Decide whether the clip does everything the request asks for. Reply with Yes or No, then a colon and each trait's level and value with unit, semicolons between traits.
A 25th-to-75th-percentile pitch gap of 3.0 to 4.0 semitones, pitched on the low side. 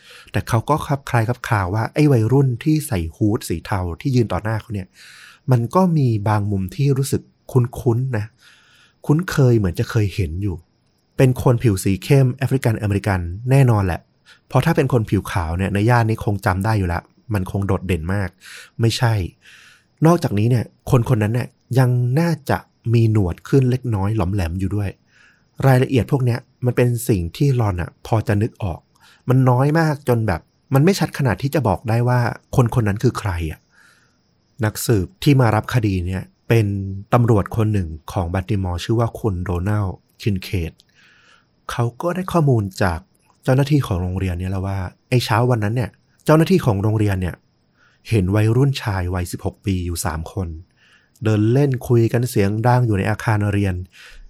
No: average, 4.5 semitones; low, 110 Hz